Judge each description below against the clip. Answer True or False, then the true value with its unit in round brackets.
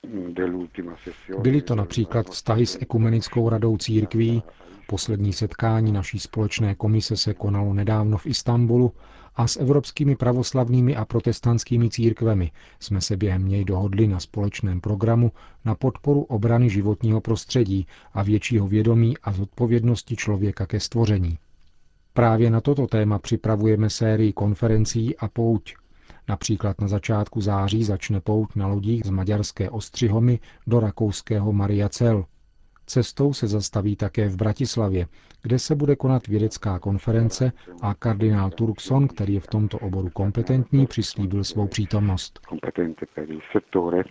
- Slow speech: False (125 wpm)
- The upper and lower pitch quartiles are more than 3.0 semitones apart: False (2.6 semitones)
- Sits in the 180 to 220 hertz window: False (110 Hz)